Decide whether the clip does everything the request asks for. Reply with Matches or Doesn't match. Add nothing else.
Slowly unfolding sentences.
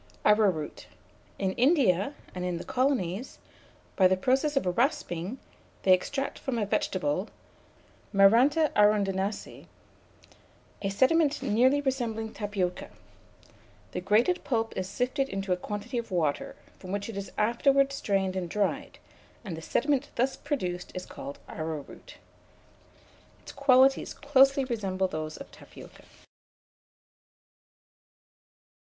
Matches